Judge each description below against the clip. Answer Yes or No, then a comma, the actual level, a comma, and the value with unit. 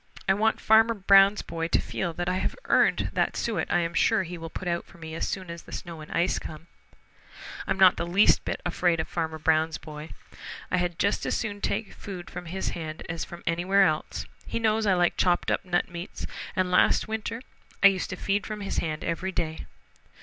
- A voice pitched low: No, medium, 175 Hz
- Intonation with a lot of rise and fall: No, average, 3.0 semitones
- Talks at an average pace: No, fast, 220 wpm